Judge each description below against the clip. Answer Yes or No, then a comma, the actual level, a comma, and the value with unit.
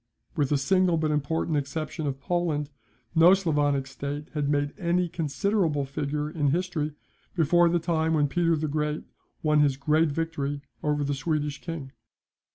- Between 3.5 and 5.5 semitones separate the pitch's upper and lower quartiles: No, narrow, 2.4 semitones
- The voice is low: No, medium, 150 Hz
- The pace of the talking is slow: No, average, 160 wpm